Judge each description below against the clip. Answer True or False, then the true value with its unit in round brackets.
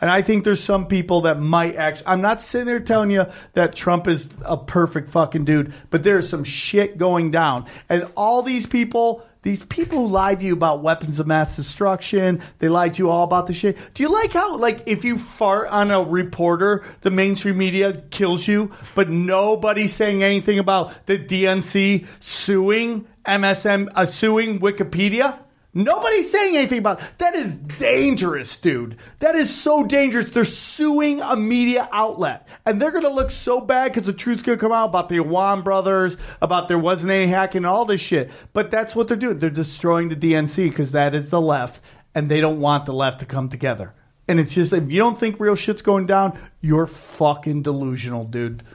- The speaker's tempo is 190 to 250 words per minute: True (195 wpm)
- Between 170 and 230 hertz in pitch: True (190 Hz)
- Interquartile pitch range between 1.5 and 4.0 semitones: False (4.9 semitones)